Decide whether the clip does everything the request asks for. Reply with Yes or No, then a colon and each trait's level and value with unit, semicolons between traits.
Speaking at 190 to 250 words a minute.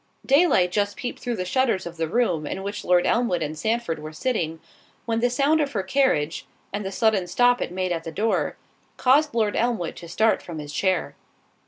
Yes: fast, 205 wpm